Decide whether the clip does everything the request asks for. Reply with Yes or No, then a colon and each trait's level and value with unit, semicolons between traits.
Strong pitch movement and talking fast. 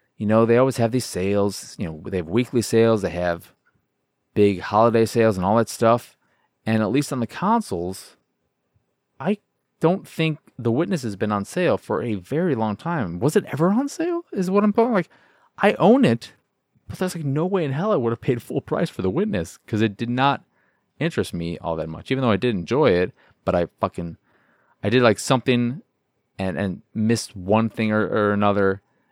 Yes: wide, 6.1 semitones; fast, 210 wpm